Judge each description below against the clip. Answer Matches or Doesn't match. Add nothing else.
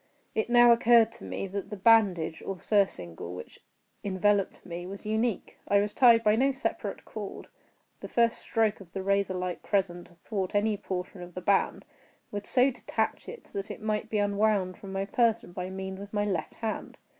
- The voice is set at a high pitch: Matches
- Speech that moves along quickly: Doesn't match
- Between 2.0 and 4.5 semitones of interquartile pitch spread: Matches